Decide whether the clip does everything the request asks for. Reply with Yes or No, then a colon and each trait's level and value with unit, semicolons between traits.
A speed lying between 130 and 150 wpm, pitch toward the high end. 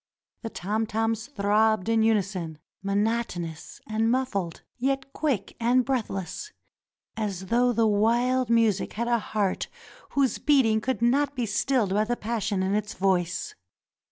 Yes: average, 140 wpm; high, 220 Hz